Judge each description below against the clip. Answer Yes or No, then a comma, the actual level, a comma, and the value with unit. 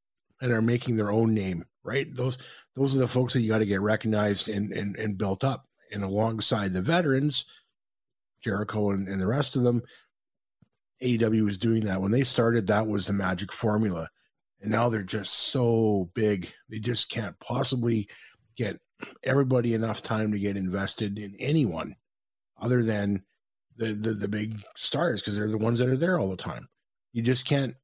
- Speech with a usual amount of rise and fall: Yes, average, 3.2 semitones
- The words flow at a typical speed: Yes, average, 180 wpm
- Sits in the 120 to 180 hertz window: No, low, 110 Hz